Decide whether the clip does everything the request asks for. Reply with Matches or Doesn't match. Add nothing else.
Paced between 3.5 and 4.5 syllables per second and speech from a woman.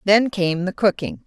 Matches